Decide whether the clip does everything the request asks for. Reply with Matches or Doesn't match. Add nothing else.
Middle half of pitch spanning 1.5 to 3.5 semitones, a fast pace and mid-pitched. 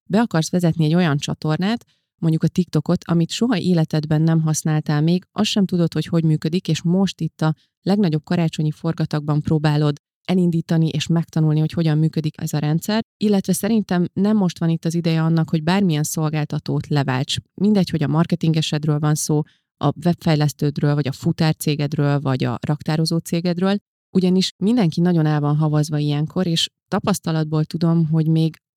Matches